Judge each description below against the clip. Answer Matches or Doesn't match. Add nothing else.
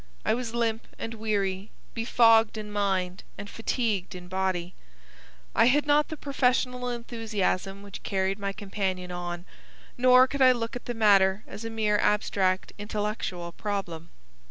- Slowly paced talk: Doesn't match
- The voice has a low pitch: Doesn't match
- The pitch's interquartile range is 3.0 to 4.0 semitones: Matches